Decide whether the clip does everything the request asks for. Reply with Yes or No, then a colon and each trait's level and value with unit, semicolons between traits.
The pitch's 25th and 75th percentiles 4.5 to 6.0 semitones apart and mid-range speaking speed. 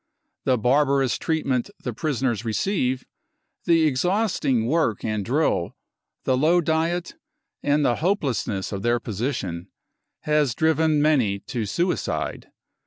No: average, 5.2 semitones; slow, 120 wpm